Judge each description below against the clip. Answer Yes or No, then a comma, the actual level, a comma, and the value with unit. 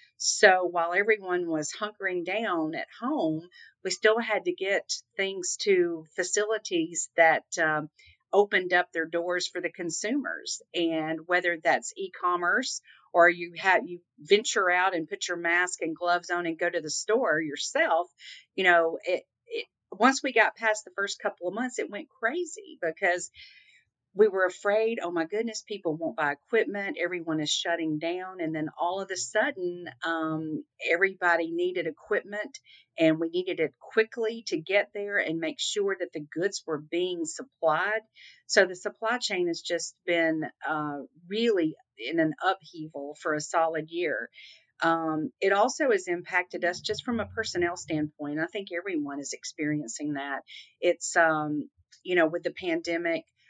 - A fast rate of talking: No, average, 165 wpm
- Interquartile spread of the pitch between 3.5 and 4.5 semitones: Yes, average, 4.2 semitones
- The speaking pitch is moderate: Yes, medium, 175 Hz